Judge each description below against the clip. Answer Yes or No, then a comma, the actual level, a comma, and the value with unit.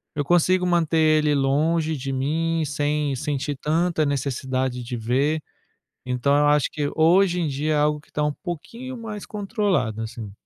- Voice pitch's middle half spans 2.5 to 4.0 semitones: Yes, average, 3.3 semitones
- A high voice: No, medium, 150 Hz